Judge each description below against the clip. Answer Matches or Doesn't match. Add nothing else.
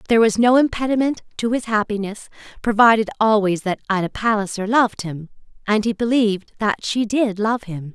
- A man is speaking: Doesn't match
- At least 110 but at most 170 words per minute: Matches